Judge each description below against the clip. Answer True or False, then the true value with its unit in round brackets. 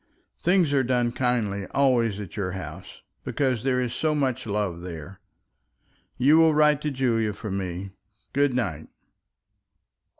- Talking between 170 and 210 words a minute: False (140 wpm)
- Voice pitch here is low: True (120 Hz)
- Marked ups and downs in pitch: True (5.7 semitones)